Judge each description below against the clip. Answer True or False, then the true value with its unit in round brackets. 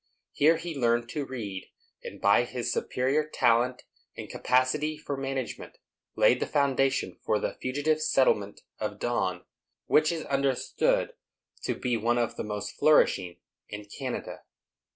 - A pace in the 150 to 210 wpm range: False (140 wpm)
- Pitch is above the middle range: False (130 Hz)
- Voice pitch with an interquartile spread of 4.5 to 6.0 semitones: False (3.8 semitones)